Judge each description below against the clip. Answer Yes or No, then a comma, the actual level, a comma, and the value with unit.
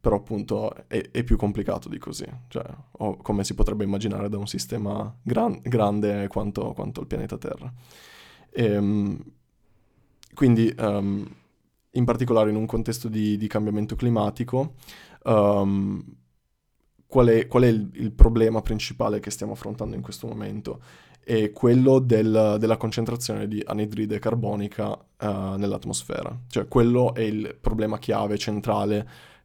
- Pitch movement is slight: Yes, narrow, 1.9 semitones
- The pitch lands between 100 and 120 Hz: Yes, low, 105 Hz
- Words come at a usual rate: Yes, average, 140 wpm